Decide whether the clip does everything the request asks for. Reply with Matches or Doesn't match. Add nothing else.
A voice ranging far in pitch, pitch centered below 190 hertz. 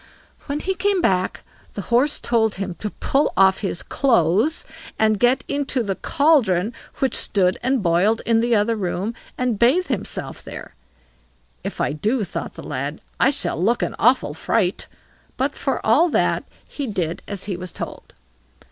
Doesn't match